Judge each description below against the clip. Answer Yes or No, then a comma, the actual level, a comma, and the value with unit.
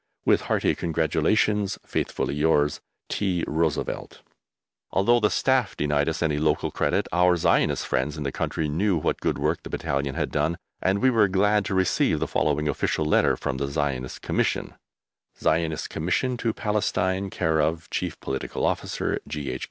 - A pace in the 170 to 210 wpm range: No, average, 160 wpm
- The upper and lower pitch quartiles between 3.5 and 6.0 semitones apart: Yes, average, 4.8 semitones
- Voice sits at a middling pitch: No, very low, 80 Hz